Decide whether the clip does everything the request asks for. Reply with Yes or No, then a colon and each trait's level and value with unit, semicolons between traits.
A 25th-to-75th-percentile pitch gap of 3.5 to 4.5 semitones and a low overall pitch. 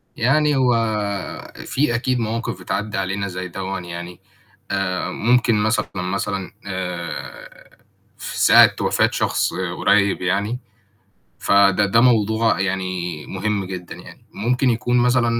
Yes: average, 4.1 semitones; low, 100 Hz